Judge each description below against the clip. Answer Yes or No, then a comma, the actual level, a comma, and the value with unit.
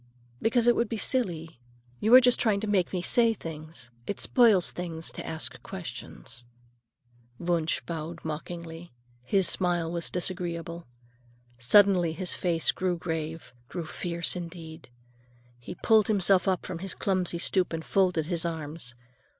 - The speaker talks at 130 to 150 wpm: Yes, average, 145 wpm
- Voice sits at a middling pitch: Yes, medium, 175 Hz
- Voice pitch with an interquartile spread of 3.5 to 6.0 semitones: No, average, 2.9 semitones